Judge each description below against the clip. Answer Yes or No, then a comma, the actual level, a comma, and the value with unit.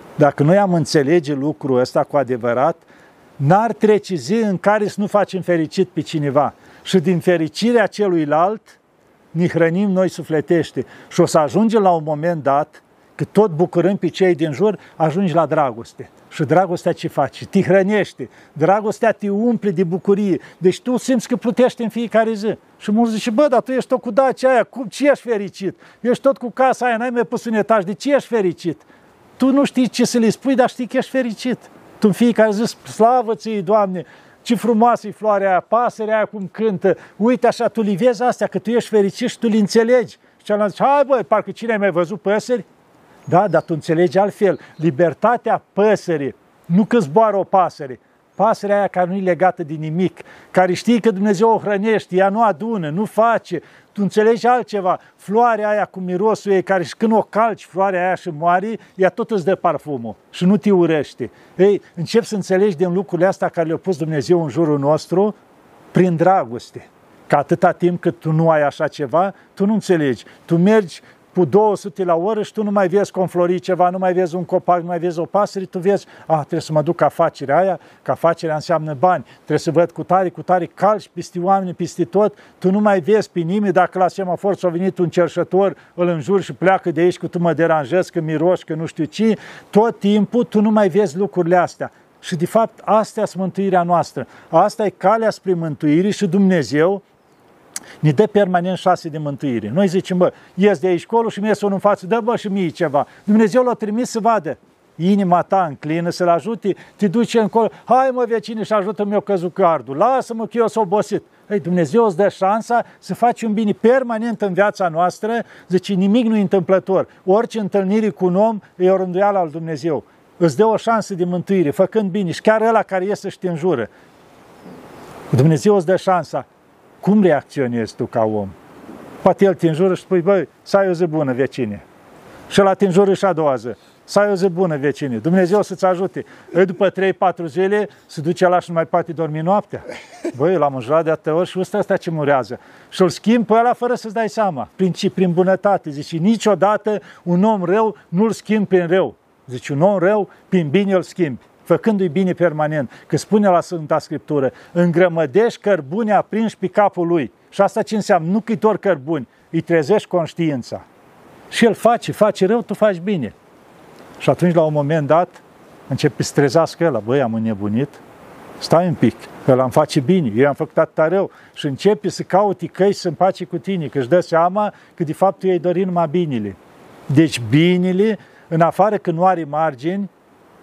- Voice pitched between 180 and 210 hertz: Yes, high, 190 Hz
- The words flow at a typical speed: No, fast, 200 wpm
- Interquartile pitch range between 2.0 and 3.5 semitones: No, average, 3.9 semitones